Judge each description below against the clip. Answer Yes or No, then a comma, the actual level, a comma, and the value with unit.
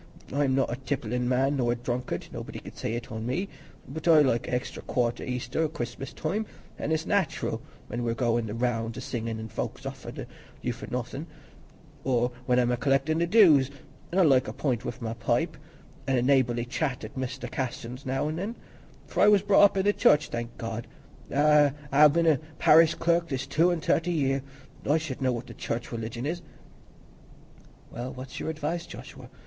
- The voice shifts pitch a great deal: No, average, 4.7 semitones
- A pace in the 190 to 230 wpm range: Yes, average, 200 wpm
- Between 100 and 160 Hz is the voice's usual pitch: Yes, low, 135 Hz